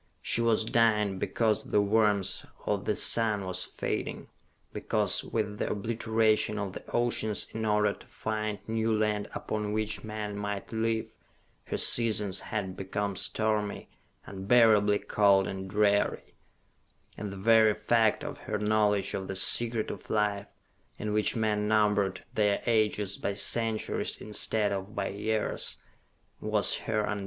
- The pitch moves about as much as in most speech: No, narrow, 1.3 semitones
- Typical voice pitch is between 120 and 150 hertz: No, low, 105 Hz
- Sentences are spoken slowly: No, average, 145 wpm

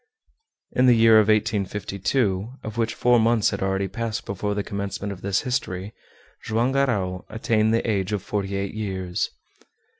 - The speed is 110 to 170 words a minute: Yes, average, 155 wpm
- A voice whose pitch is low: Yes, low, 105 Hz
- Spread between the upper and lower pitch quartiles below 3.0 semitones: Yes, narrow, 2.6 semitones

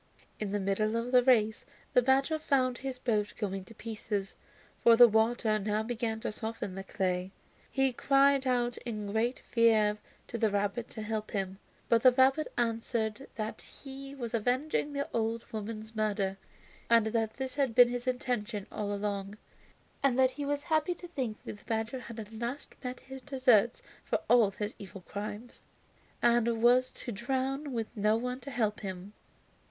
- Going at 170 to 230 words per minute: Yes, average, 175 wpm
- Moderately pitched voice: No, high, 230 Hz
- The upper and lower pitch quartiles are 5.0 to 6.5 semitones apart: No, average, 3.2 semitones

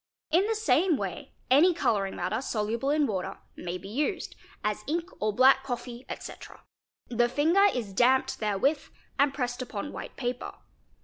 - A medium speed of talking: Yes, average, 160 wpm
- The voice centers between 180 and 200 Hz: No, very high, 250 Hz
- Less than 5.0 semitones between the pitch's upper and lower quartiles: No, wide, 5.6 semitones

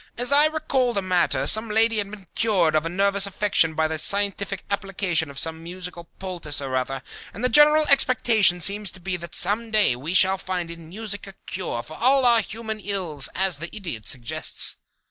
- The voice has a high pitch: Yes, high, 195 Hz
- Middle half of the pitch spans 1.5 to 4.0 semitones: No, average, 4.5 semitones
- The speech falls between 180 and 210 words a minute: Yes, average, 200 wpm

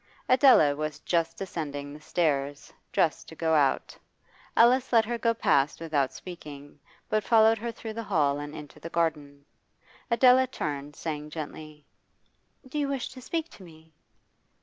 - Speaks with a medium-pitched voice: Yes, medium, 160 Hz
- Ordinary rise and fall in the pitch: No, wide, 7.6 semitones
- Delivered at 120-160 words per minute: Yes, average, 155 wpm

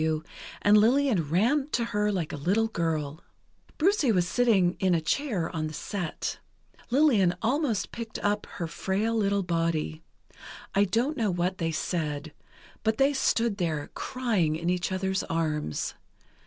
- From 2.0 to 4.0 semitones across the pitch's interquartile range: No, wide, 5.6 semitones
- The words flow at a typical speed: Yes, average, 155 wpm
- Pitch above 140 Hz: Yes, high, 190 Hz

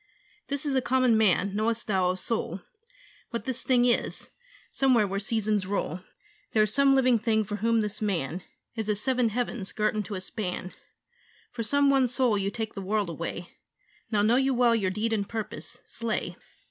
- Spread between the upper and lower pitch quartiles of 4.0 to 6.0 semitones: No, average, 3.4 semitones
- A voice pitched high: Yes, high, 220 Hz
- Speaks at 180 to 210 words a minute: Yes, average, 185 wpm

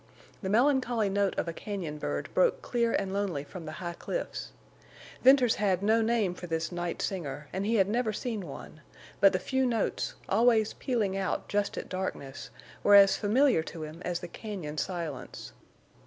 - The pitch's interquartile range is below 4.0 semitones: No, average, 4.6 semitones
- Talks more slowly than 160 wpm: No, average, 180 wpm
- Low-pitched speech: No, high, 195 Hz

